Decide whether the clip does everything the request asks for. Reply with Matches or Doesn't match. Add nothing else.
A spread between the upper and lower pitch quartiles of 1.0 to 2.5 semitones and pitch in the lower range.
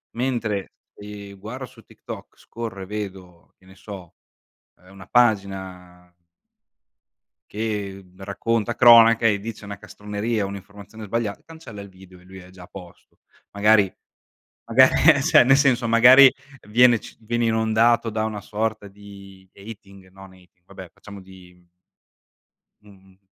Doesn't match